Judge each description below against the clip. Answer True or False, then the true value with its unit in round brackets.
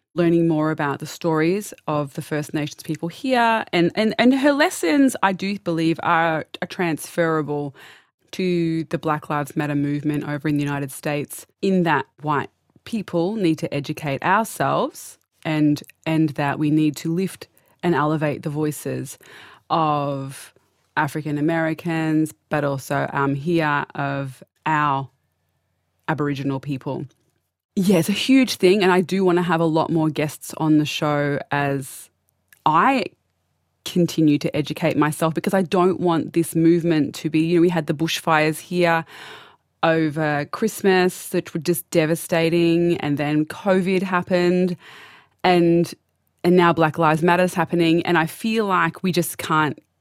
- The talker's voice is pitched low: False (160 Hz)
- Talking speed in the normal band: True (150 wpm)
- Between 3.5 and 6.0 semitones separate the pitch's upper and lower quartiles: False (2.9 semitones)